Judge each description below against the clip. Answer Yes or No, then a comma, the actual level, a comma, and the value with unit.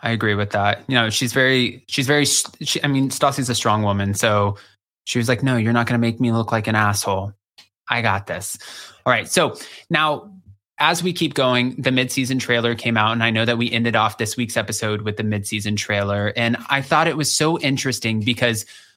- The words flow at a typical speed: No, fast, 220 wpm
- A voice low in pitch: Yes, low, 120 Hz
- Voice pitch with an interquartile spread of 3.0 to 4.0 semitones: Yes, average, 3.7 semitones